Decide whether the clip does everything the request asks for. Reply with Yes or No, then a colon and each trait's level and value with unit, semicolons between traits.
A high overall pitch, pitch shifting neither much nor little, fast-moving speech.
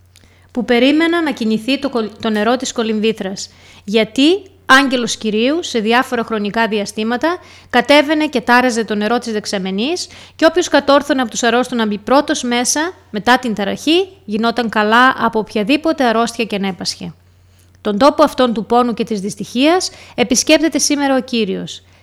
No: high, 240 Hz; average, 4.5 semitones; average, 150 wpm